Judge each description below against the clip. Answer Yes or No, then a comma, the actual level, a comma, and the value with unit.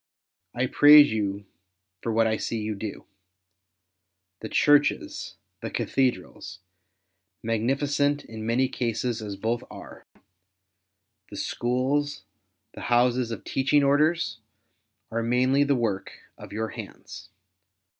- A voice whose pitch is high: No, low, 115 Hz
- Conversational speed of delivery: No, slow, 125 wpm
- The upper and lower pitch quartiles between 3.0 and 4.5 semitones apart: Yes, average, 4.0 semitones